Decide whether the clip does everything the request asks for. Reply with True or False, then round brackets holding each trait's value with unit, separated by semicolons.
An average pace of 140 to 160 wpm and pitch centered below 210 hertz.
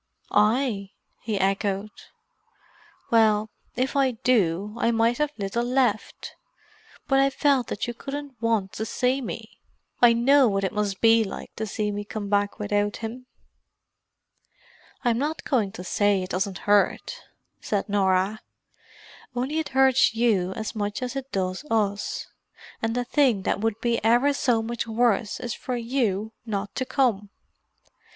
False (155 wpm; 225 Hz)